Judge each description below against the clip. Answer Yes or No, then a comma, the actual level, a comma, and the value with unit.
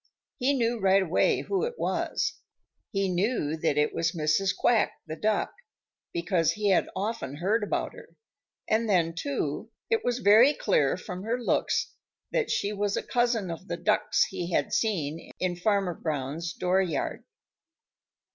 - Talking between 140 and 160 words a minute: Yes, average, 155 wpm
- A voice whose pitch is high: Yes, high, 195 Hz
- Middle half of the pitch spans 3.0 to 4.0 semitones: No, average, 5.0 semitones